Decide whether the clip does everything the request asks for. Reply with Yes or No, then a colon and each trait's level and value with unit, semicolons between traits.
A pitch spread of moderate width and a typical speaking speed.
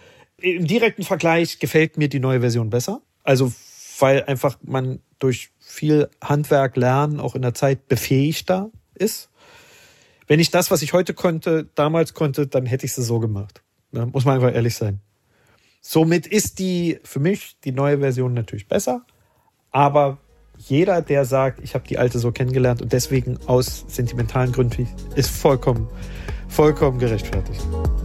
Yes: average, 4.2 semitones; average, 155 wpm